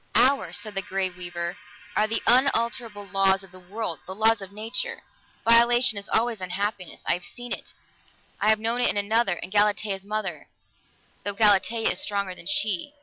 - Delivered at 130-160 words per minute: No, average, 180 wpm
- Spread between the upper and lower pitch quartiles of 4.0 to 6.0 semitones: No, average, 2.9 semitones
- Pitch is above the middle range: Yes, high, 205 Hz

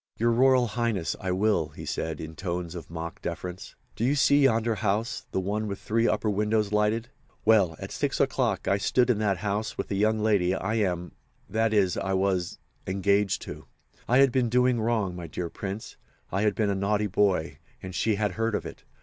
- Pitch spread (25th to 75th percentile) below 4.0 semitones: Yes, average, 3.1 semitones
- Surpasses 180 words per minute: Yes, average, 190 wpm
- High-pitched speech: No, low, 105 Hz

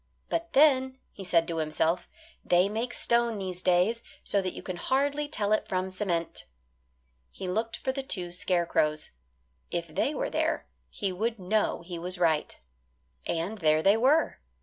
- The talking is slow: No, average, 165 wpm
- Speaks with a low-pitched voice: No, high, 190 Hz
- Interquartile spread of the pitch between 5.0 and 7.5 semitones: Yes, average, 5.3 semitones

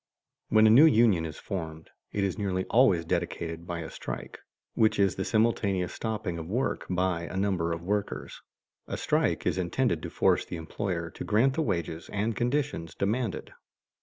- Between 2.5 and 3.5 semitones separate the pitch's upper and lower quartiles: No, average, 4.6 semitones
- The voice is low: Yes, very low, 95 Hz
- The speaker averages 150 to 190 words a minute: Yes, average, 175 wpm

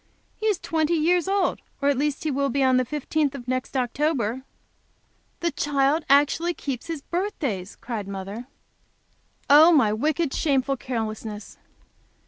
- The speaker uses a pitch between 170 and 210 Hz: No, very high, 280 Hz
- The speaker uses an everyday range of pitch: Yes, average, 4.2 semitones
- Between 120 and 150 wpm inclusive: Yes, average, 145 wpm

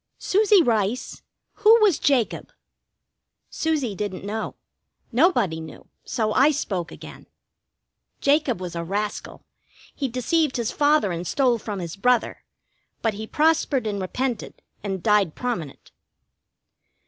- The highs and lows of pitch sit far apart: Yes, wide, 6.5 semitones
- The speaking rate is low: Yes, slow, 125 wpm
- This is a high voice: Yes, high, 230 Hz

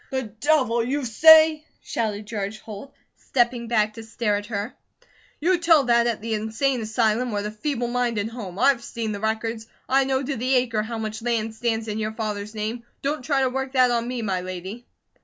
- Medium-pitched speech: No, high, 230 Hz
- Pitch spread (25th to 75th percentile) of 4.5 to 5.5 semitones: No, average, 3.0 semitones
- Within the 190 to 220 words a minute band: Yes, average, 200 wpm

